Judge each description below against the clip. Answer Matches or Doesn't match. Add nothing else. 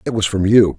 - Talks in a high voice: Doesn't match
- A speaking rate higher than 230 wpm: Matches